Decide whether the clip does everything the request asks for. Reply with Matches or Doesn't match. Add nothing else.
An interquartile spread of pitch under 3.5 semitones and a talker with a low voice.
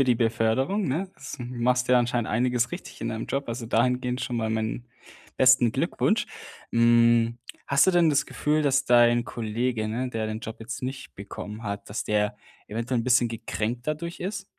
Matches